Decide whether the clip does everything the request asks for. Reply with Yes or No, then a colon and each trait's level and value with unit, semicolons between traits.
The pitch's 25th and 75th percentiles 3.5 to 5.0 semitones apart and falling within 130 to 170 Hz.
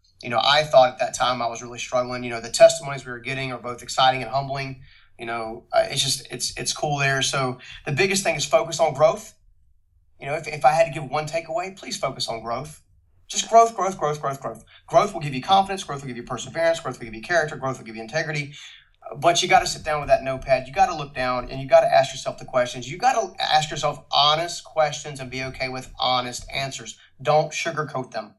Yes: average, 4.7 semitones; low, 135 Hz